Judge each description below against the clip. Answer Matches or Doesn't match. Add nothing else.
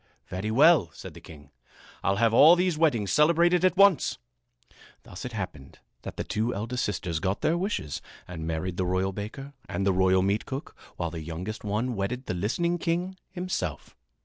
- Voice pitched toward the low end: Matches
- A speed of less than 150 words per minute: Doesn't match